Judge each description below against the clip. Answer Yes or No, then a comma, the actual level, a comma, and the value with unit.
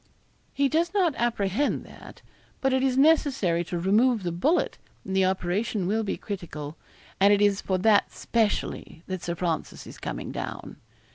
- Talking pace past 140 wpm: Yes, average, 165 wpm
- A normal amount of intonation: No, wide, 6.2 semitones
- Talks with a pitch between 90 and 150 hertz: No, high, 205 Hz